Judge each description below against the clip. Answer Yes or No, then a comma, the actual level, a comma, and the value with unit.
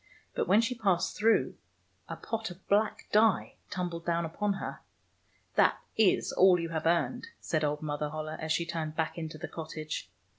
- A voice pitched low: No, medium, 170 Hz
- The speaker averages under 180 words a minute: No, average, 185 wpm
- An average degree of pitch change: Yes, average, 4.2 semitones